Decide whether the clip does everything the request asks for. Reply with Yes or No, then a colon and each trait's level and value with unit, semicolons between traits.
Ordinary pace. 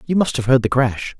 No: fast, 305 wpm